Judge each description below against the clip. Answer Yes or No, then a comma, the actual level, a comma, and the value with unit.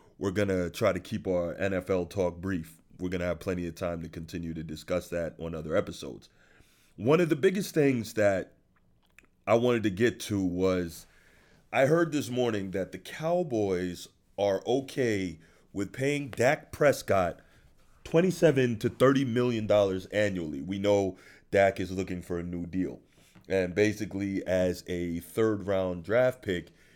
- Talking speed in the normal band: Yes, average, 160 wpm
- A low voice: Yes, very low, 95 Hz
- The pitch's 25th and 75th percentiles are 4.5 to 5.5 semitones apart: Yes, average, 4.8 semitones